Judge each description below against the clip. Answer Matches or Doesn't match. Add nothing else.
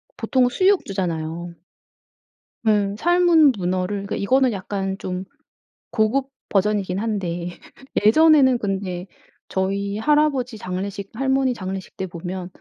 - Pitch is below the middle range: Doesn't match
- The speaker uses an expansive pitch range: Matches